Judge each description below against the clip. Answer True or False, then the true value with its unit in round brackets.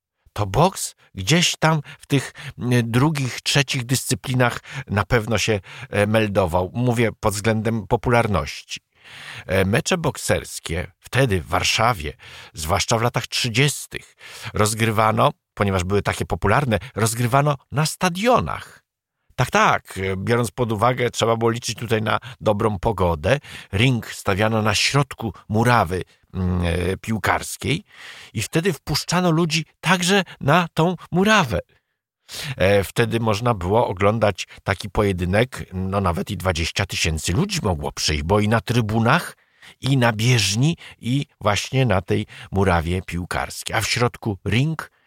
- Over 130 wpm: False (125 wpm)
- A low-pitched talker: True (115 Hz)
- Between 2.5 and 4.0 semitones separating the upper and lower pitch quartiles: False (4.7 semitones)